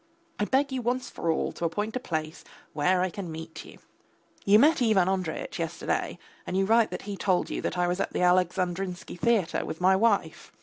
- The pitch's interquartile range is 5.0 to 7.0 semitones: No, average, 3.5 semitones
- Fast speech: Yes, fast, 210 wpm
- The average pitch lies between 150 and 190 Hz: Yes, medium, 185 Hz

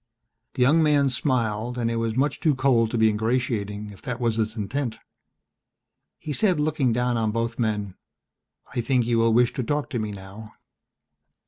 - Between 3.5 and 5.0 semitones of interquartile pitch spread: No, average, 2.9 semitones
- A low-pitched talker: Yes, low, 120 Hz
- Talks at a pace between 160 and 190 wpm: Yes, average, 185 wpm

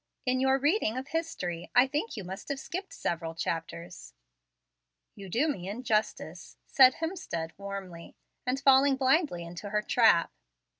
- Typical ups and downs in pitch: No, wide, 7.5 semitones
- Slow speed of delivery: No, average, 145 wpm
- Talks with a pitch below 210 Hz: No, high, 225 Hz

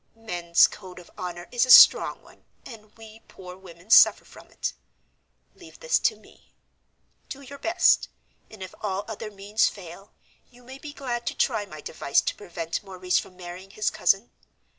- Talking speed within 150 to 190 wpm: Yes, average, 175 wpm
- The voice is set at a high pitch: Yes, high, 200 Hz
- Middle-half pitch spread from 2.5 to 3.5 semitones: No, average, 4.7 semitones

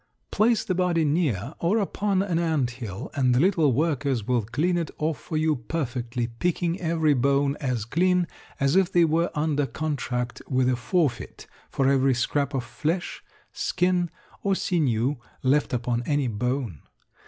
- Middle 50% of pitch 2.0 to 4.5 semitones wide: No, average, 5.2 semitones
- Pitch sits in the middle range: Yes, medium, 145 Hz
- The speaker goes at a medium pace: Yes, average, 160 wpm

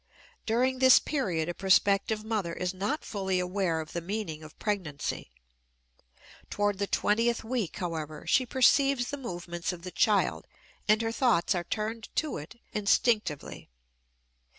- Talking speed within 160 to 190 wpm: No, average, 145 wpm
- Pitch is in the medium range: No, high, 205 Hz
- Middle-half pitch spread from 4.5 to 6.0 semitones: Yes, average, 4.9 semitones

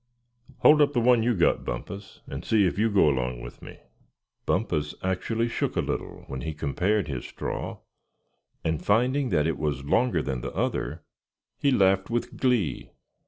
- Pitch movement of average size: No, wide, 7.8 semitones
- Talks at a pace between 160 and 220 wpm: Yes, average, 170 wpm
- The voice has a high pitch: No, very low, 95 Hz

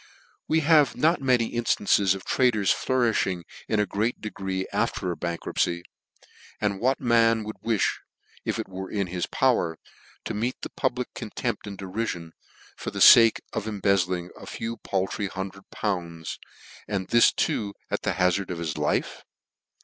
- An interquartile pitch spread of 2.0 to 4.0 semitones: Yes, average, 3.7 semitones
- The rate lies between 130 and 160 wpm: Yes, average, 155 wpm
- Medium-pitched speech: No, low, 100 Hz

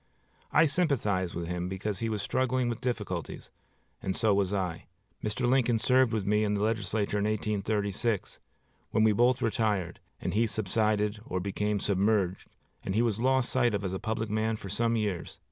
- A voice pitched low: Yes, low, 105 Hz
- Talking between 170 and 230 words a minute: Yes, average, 180 wpm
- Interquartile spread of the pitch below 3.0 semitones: Yes, narrow, 2.6 semitones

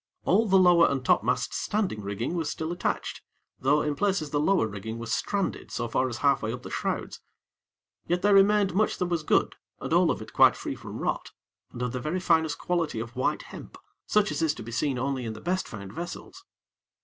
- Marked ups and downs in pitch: Yes, wide, 6.9 semitones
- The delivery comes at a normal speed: No, fast, 220 wpm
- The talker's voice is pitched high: No, medium, 150 Hz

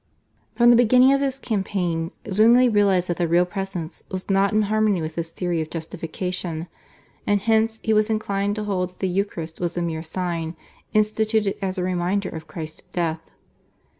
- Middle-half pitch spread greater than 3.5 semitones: Yes, average, 3.9 semitones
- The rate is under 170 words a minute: No, average, 180 wpm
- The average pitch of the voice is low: No, high, 190 Hz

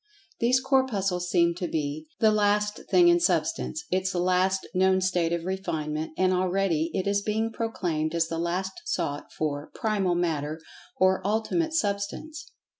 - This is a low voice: No, medium, 185 Hz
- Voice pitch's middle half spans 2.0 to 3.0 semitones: No, average, 3.9 semitones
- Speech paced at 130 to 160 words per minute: Yes, average, 145 wpm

